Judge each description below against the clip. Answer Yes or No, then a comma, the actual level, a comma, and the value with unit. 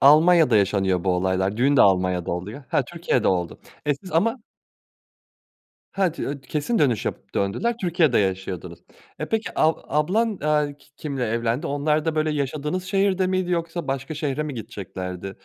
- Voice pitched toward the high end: No, medium, 145 Hz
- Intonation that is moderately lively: No, wide, 8.8 semitones